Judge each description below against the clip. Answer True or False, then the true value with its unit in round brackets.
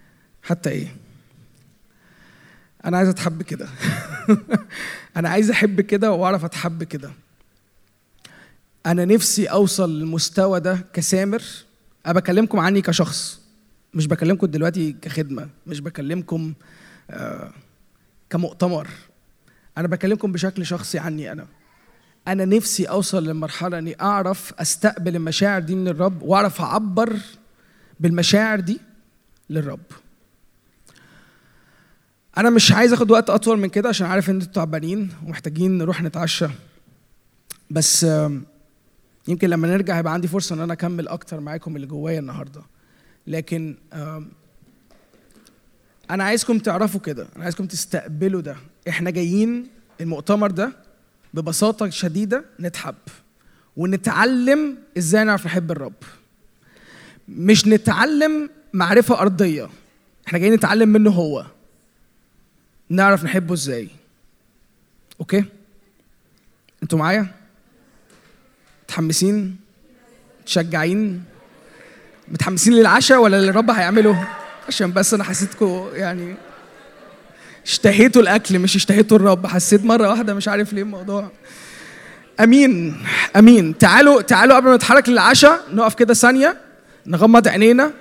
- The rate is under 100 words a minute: False (105 wpm)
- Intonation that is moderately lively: True (4.3 semitones)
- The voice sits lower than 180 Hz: False (190 Hz)